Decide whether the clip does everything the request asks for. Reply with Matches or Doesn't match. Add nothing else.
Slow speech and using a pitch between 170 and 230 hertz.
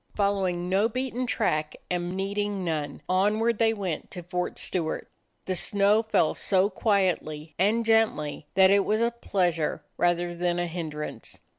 Doesn't match